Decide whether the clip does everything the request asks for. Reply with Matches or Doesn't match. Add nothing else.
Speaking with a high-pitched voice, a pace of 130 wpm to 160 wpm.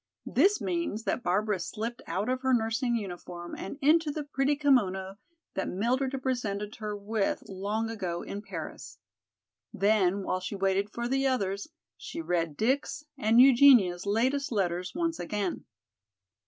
Matches